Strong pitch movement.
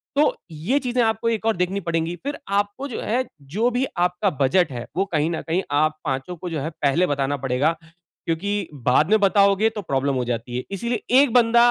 Yes: wide, 7.3 semitones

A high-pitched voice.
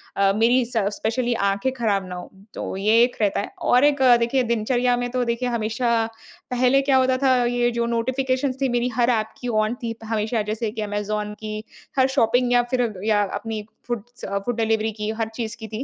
Yes: high, 235 Hz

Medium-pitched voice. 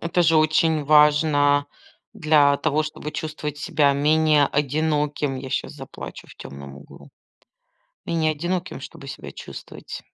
Yes: medium, 150 Hz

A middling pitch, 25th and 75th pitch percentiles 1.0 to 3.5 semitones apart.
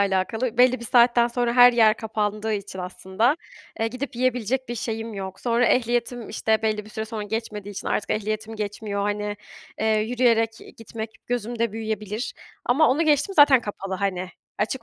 No: high, 225 Hz; narrow, 2.5 semitones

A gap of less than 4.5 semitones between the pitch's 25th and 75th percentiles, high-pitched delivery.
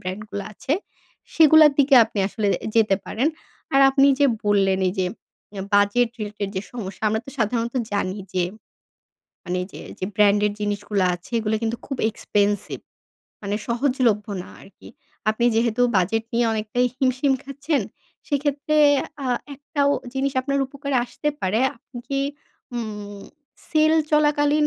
No: average, 5.2 semitones; high, 230 Hz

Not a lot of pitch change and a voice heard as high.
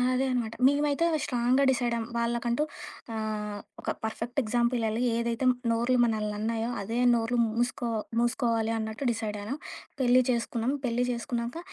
Yes: narrow, 1.7 semitones; high, 235 Hz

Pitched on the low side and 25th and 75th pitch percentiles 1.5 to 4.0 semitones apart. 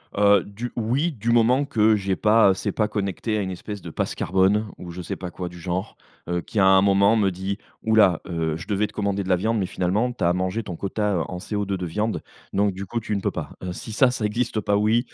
Yes: low, 100 Hz; average, 2.9 semitones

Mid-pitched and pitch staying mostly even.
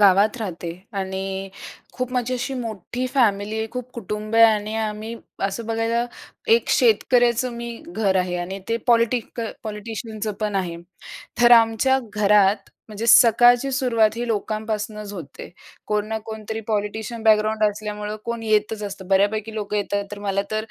No: high, 215 Hz; narrow, 2.2 semitones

